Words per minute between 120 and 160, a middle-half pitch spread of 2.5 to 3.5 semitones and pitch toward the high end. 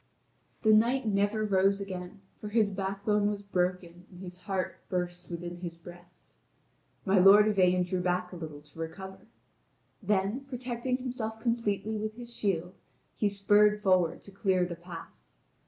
Yes: average, 155 wpm; average, 2.9 semitones; high, 195 Hz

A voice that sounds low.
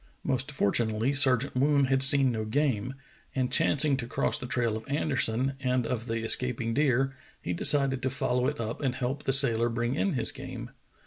Yes: low, 130 Hz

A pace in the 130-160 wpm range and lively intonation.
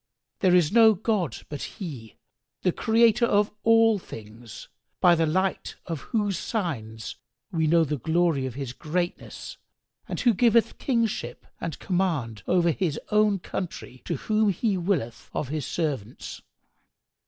Yes: average, 140 wpm; wide, 6.3 semitones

